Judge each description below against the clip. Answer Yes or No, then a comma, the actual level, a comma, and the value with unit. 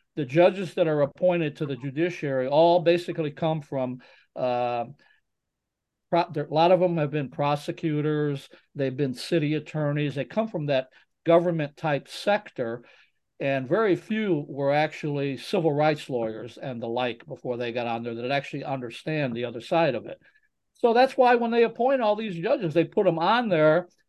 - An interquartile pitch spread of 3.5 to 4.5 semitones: Yes, average, 4.2 semitones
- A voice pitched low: No, medium, 150 Hz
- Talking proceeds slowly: No, average, 175 wpm